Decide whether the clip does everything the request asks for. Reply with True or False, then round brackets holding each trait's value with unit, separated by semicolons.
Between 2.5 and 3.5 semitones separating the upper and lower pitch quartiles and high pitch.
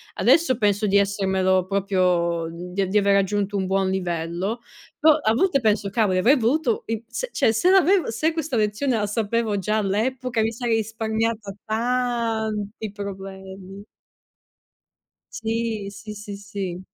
True (2.9 semitones; 210 Hz)